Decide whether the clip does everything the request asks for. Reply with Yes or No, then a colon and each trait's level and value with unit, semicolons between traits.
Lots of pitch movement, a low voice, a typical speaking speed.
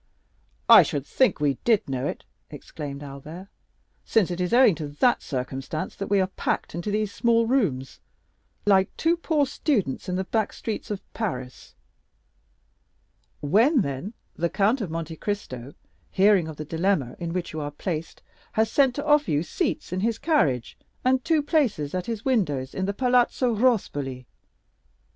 No: wide, 7.7 semitones; high, 190 Hz; average, 165 wpm